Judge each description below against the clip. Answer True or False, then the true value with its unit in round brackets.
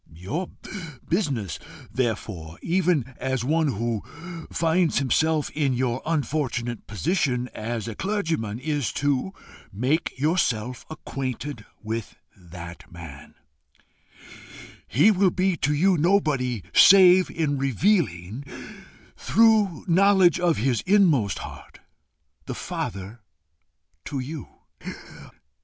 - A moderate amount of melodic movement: False (6.8 semitones)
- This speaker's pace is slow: True (100 wpm)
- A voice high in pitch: False (140 Hz)